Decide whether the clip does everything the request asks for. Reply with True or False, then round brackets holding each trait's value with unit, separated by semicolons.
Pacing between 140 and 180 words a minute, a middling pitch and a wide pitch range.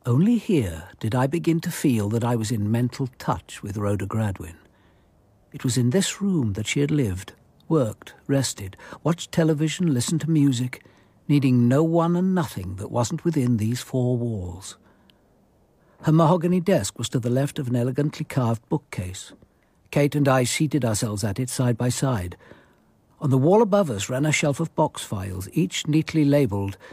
False (175 wpm; 130 Hz; 6.0 semitones)